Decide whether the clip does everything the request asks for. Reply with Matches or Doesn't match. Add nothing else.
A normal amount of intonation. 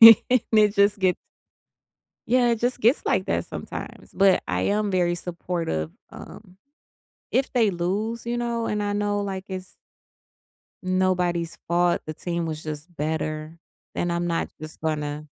Matches